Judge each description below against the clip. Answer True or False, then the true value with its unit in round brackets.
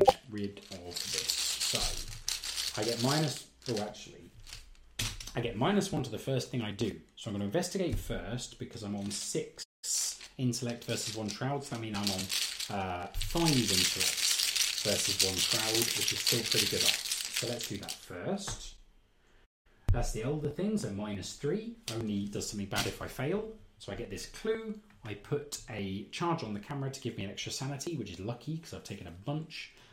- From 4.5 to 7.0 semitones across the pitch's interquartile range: True (5.1 semitones)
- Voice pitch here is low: True (110 Hz)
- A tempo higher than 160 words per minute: True (190 wpm)